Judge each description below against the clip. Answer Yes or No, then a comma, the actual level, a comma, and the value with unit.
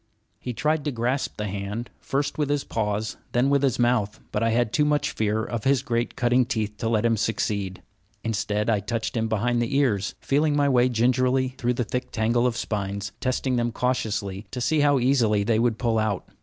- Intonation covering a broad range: No, average, 3.2 semitones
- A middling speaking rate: No, fast, 210 wpm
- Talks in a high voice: No, low, 120 Hz